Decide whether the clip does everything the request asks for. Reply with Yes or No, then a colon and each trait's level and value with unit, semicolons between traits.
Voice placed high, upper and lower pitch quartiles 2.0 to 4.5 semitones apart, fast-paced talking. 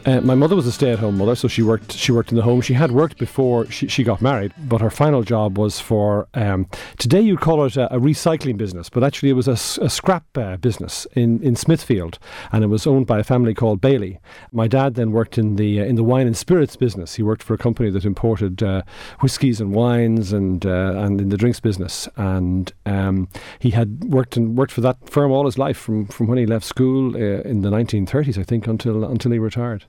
No: low, 115 Hz; average, 3.7 semitones; fast, 240 wpm